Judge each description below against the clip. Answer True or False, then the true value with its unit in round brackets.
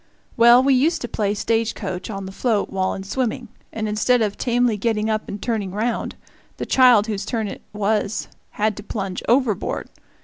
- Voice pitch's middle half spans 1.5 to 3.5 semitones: True (2.8 semitones)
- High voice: True (215 Hz)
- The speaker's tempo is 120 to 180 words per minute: False (190 wpm)